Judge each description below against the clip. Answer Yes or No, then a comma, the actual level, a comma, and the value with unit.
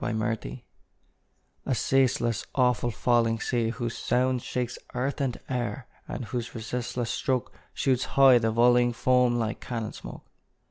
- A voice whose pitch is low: Yes, low, 120 Hz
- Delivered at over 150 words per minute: No, slow, 135 wpm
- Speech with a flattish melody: Yes, narrow, 1.6 semitones